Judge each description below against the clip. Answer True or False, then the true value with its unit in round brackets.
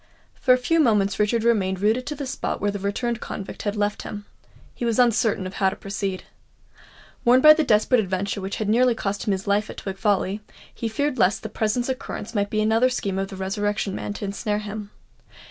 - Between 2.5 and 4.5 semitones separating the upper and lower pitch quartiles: True (2.9 semitones)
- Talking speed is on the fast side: True (215 wpm)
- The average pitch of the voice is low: False (210 Hz)